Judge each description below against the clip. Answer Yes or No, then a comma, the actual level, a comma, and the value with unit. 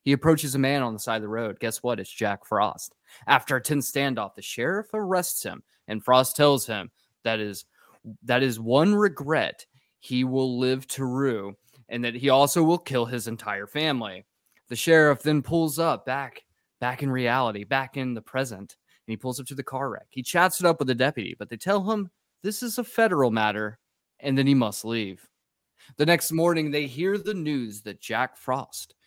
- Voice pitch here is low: Yes, low, 130 Hz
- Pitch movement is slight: No, average, 4.9 semitones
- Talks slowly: No, fast, 205 wpm